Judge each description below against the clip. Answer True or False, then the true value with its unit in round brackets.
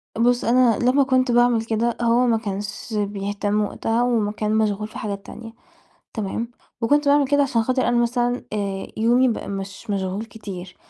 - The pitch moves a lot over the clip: False (2.9 semitones)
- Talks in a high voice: True (225 Hz)